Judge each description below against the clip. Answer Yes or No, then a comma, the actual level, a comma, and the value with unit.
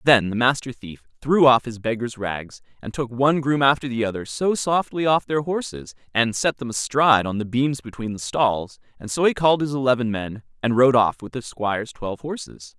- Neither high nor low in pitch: No, low, 125 Hz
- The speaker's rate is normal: No, fast, 215 wpm